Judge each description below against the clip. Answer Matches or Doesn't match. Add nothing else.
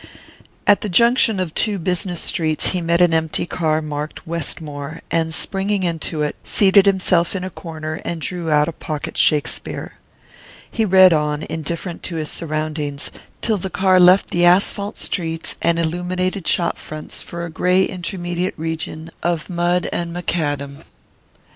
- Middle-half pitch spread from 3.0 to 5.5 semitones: Doesn't match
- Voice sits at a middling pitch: Matches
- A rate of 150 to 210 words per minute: Matches